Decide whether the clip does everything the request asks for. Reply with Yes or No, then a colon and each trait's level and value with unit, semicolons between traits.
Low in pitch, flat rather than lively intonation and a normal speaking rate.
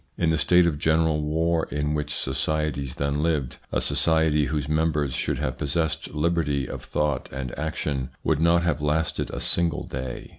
Yes: very low, 75 Hz; narrow, 2.1 semitones; average, 175 wpm